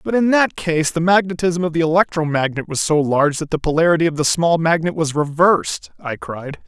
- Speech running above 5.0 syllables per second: Yes, 5.6 syllables/s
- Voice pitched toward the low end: No, medium, 165 Hz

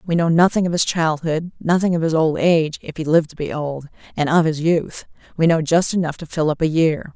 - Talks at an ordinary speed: No, fast, 250 wpm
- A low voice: No, medium, 160 Hz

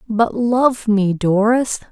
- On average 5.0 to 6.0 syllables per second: No, 3.0 syllables/s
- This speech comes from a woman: Yes, female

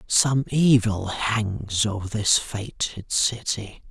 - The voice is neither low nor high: No, low, 110 Hz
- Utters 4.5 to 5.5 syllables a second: No, 3.0 syllables/s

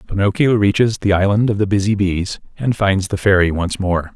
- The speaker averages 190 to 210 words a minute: Yes, average, 200 wpm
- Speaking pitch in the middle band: No, low, 100 Hz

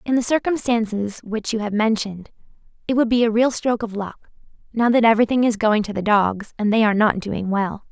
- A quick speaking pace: Yes, fast, 220 wpm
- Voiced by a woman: Yes, female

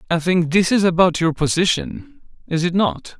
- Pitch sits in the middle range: Yes, medium, 180 Hz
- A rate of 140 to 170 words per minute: No, average, 190 wpm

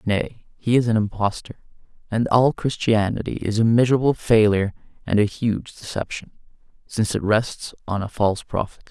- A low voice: Yes, low, 110 Hz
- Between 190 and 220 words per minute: No, average, 155 wpm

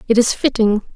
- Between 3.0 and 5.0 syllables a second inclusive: No, 5.5 syllables/s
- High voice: Yes, high, 225 Hz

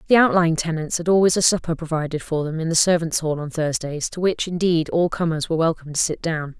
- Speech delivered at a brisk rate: Yes, fast, 235 wpm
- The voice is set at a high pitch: No, medium, 165 Hz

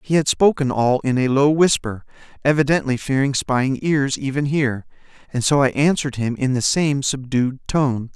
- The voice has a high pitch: No, low, 135 Hz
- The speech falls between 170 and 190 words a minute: Yes, average, 175 wpm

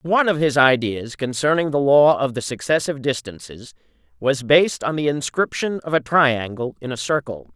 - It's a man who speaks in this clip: Yes, male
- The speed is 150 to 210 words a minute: Yes, average, 175 wpm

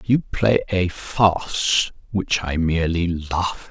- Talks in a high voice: No, very low, 90 Hz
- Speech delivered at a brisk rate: No, average, 145 wpm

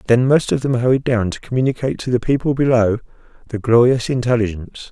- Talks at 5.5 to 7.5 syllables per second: Yes, 6.4 syllables/s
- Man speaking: Yes, male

